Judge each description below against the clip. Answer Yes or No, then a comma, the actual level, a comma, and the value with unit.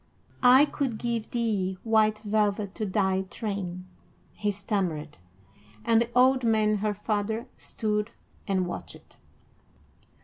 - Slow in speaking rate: Yes, slow, 115 wpm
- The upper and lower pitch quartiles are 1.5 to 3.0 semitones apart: Yes, narrow, 2.5 semitones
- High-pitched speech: Yes, high, 210 Hz